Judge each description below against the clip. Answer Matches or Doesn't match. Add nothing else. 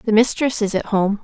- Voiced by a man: Doesn't match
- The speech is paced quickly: Matches